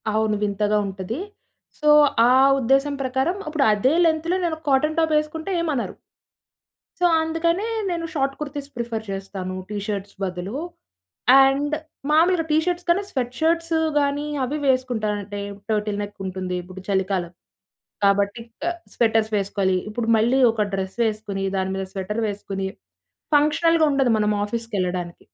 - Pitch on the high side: Yes, high, 230 Hz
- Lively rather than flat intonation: Yes, wide, 7.1 semitones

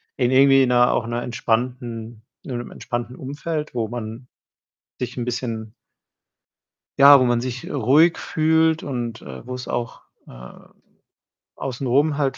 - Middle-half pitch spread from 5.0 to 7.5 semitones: No, narrow, 2.6 semitones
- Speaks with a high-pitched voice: No, low, 125 Hz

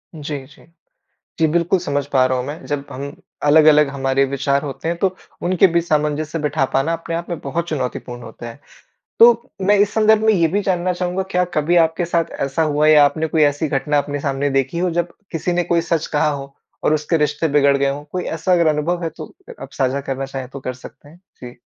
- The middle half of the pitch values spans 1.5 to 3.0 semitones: No, average, 3.5 semitones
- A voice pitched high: No, medium, 150 Hz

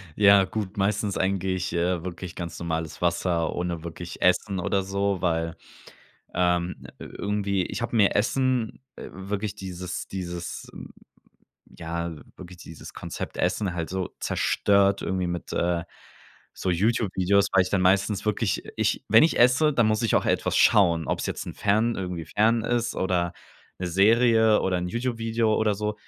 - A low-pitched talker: Yes, very low, 95 Hz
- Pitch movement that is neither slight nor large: Yes, average, 3.4 semitones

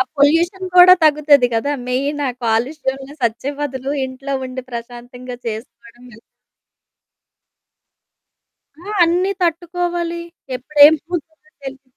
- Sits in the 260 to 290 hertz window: Yes, very high, 280 Hz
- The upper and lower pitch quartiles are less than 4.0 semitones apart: No, average, 4.8 semitones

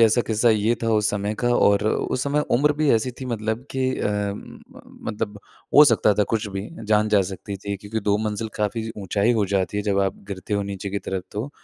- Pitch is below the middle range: Yes, low, 105 Hz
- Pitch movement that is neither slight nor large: No, narrow, 2.1 semitones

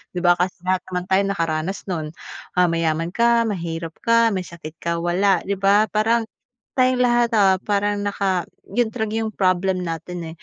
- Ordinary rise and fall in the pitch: Yes, average, 3.9 semitones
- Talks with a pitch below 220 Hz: Yes, high, 190 Hz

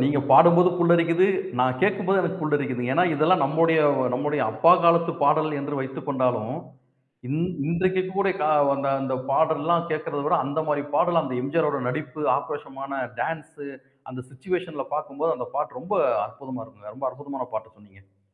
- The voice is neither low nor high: Yes, medium, 150 Hz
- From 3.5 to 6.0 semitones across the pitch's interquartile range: Yes, average, 4.0 semitones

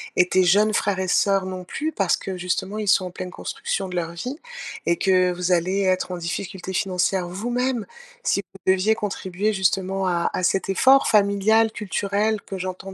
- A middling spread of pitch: No, narrow, 2.2 semitones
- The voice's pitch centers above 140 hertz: Yes, high, 190 Hz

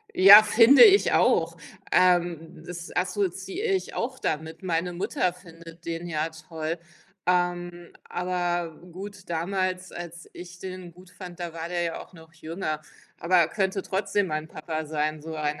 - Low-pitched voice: No, medium, 175 Hz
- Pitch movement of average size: No, narrow, 2.3 semitones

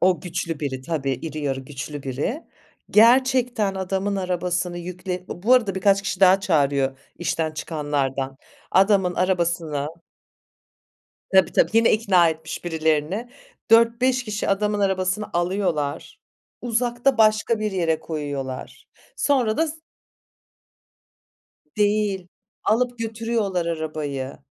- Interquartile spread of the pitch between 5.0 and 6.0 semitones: Yes, wide, 5.4 semitones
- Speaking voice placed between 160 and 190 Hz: Yes, medium, 185 Hz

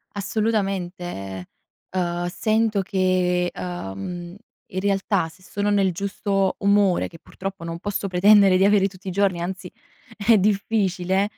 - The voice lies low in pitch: No, high, 190 Hz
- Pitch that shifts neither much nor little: No, narrow, 2.1 semitones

